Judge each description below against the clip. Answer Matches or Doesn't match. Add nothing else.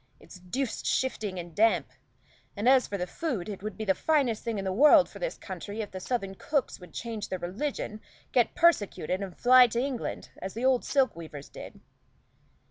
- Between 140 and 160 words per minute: Doesn't match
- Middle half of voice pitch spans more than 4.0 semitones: Matches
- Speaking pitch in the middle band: Doesn't match